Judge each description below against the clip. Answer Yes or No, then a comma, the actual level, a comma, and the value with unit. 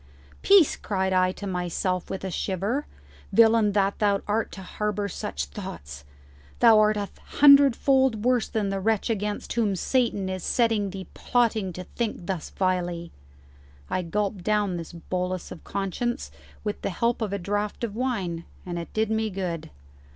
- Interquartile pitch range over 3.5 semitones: No, average, 3.2 semitones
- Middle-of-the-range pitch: No, high, 200 Hz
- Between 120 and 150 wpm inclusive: No, average, 165 wpm